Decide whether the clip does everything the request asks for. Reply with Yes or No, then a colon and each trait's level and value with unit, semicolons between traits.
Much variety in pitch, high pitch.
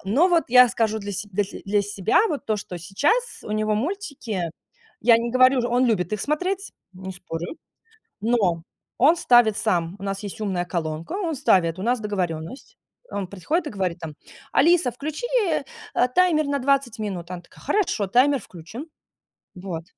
Yes: wide, 6.9 semitones; high, 215 Hz